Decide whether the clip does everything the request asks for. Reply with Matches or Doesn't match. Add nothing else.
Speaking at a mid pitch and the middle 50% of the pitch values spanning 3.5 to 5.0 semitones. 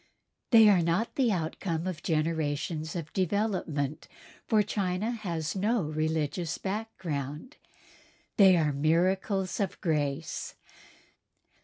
Matches